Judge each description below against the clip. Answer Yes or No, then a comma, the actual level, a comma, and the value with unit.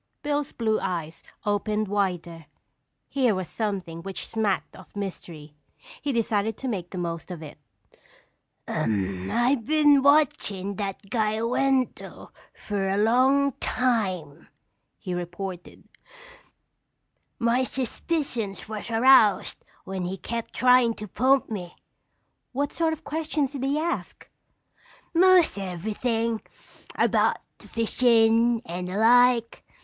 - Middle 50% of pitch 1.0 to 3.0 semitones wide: No, average, 5.2 semitones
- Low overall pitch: No, high, 220 Hz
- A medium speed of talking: No, slow, 115 wpm